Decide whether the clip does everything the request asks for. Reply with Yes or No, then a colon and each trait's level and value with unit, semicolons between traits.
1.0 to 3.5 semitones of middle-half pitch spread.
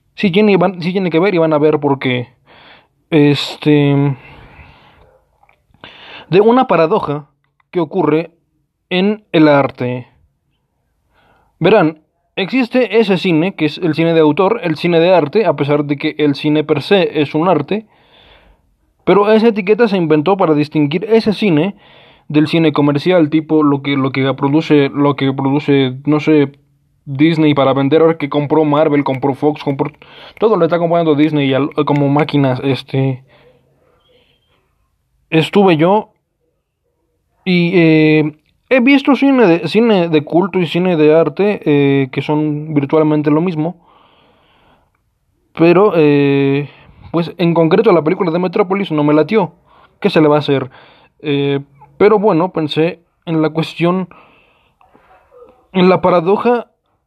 No: average, 3.9 semitones